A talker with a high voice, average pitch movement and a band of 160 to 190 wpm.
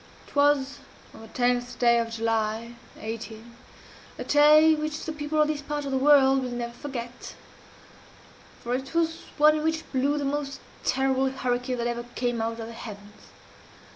Yes: very high, 260 Hz; average, 3.7 semitones; average, 170 wpm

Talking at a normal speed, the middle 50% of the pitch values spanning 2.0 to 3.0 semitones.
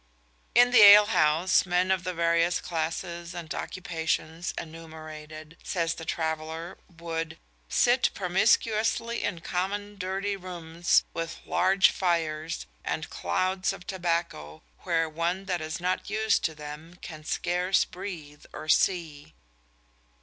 No: slow, 125 wpm; average, 2.7 semitones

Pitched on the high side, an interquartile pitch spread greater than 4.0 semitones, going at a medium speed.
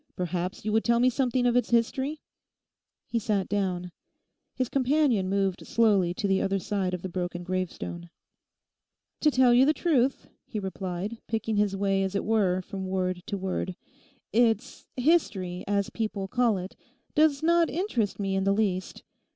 Yes: high, 205 Hz; average, 4.6 semitones; average, 165 wpm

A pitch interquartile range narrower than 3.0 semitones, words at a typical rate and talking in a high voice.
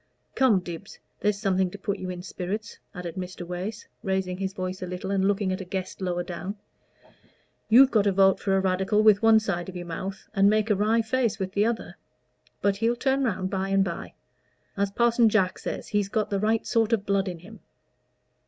No: narrow, 2.5 semitones; fast, 210 wpm; high, 195 Hz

